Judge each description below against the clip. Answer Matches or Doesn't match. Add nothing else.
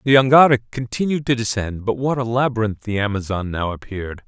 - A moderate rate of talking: Matches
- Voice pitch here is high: Doesn't match